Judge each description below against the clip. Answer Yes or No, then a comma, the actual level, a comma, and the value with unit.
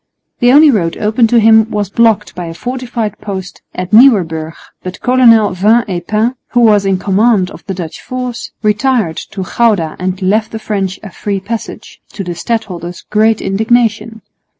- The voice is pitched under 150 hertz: No, high, 210 Hz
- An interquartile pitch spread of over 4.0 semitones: No, average, 3.7 semitones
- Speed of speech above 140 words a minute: Yes, average, 175 wpm